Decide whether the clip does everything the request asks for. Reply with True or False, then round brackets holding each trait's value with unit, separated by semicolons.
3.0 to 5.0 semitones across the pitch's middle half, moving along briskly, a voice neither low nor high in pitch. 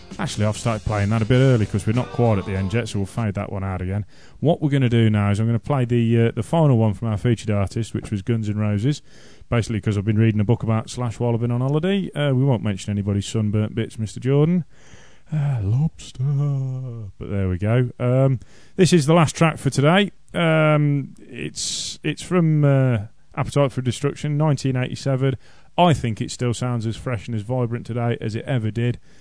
False (4.4 semitones; 225 wpm; 120 Hz)